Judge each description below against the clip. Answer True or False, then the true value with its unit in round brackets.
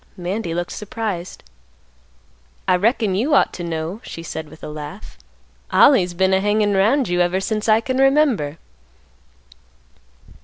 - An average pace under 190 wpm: True (145 wpm)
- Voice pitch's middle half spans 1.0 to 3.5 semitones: False (4.1 semitones)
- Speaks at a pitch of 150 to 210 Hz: True (190 Hz)